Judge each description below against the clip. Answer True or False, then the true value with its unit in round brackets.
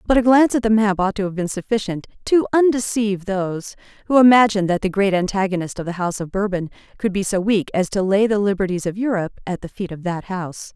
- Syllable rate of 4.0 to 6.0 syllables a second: False (6.5 syllables/s)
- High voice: True (200 Hz)